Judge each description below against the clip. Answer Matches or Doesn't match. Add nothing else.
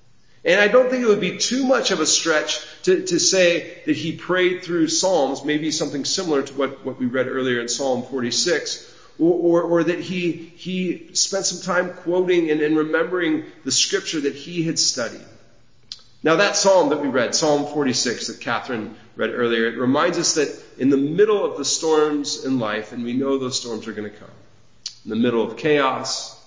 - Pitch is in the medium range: Matches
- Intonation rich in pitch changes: Matches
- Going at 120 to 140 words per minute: Doesn't match